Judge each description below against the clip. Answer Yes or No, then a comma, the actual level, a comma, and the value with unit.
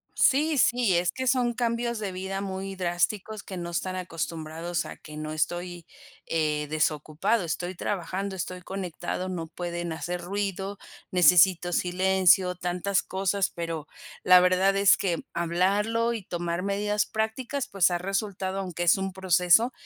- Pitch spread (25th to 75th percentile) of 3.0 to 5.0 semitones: No, narrow, 2.5 semitones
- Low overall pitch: No, medium, 185 Hz